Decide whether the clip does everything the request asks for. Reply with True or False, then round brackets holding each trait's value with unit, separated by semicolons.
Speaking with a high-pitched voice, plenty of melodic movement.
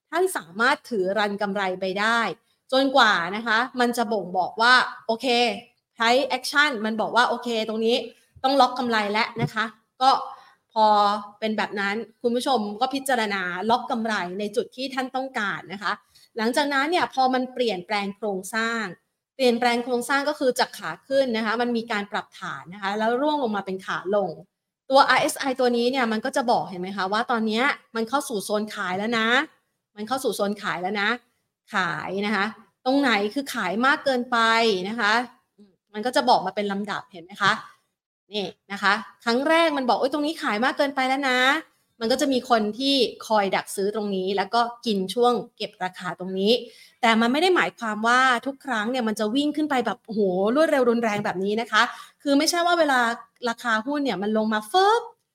False (230 Hz; 3.9 semitones)